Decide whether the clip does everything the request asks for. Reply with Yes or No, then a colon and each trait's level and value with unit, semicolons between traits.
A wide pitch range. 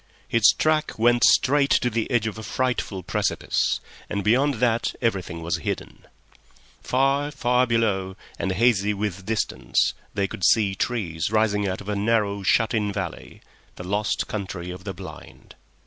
No: average, 3.7 semitones